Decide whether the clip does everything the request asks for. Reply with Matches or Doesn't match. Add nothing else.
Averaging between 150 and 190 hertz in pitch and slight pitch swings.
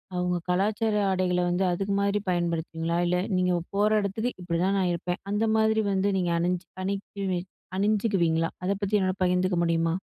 Matches